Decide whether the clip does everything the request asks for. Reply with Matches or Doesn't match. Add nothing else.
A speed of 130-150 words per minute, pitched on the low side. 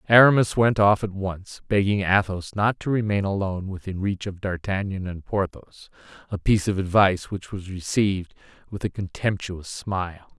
Doesn't match